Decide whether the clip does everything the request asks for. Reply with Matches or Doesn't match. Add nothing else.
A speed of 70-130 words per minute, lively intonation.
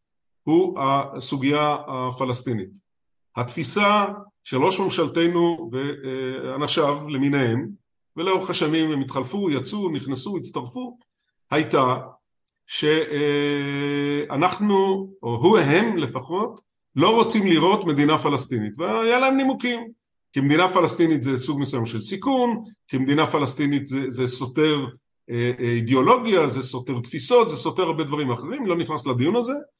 Matches